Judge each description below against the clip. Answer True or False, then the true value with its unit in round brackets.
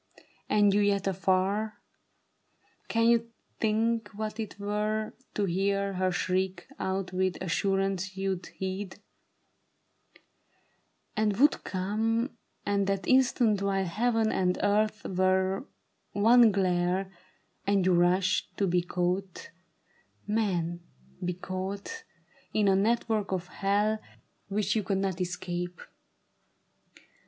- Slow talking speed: True (110 wpm)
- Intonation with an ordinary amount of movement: False (2.3 semitones)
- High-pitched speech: True (195 Hz)